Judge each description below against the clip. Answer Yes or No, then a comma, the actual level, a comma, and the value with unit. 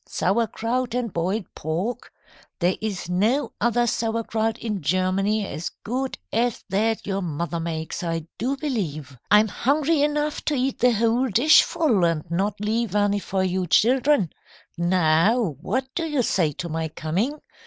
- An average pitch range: No, wide, 5.7 semitones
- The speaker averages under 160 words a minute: Yes, average, 150 wpm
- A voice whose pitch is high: Yes, high, 210 Hz